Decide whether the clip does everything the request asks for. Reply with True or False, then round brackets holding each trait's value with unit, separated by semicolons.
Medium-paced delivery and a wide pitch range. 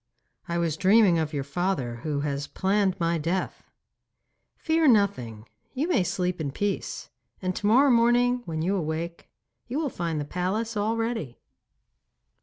True (155 wpm; 6.0 semitones)